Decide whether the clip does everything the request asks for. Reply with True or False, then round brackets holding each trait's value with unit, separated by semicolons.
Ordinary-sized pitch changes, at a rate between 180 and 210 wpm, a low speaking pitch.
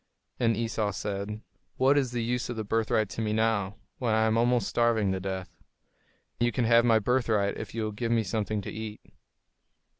False (2.0 semitones; 200 wpm; 110 Hz)